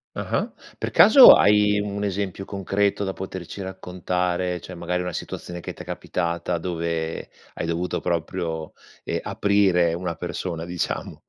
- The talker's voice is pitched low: Yes, very low, 90 Hz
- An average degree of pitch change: No, narrow, 2.3 semitones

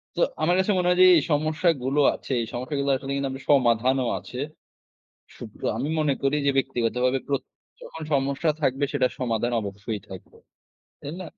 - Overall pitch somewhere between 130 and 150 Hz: Yes, low, 135 Hz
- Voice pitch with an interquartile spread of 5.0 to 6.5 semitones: No, average, 3.0 semitones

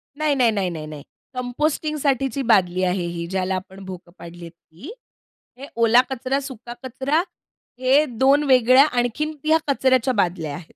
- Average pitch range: No, wide, 6.7 semitones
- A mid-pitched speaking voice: No, high, 245 Hz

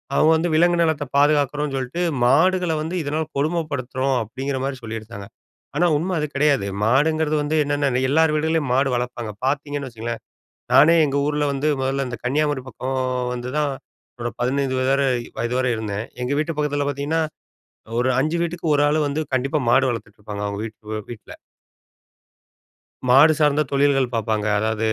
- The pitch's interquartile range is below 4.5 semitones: Yes, average, 3.5 semitones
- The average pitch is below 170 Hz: Yes, medium, 140 Hz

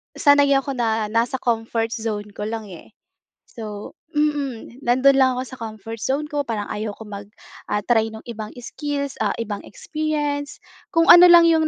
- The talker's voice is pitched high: Yes, high, 240 Hz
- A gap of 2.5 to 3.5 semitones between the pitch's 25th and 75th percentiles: No, average, 4.7 semitones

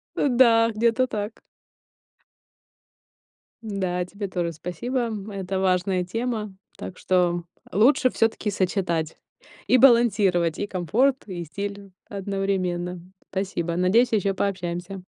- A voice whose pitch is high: Yes, high, 195 Hz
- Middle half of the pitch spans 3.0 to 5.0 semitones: Yes, average, 3.9 semitones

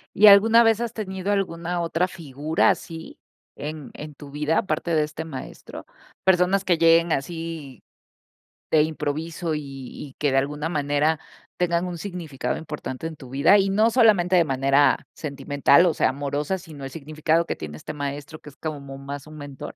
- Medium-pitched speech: Yes, medium, 155 Hz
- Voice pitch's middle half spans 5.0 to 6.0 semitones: No, average, 3.6 semitones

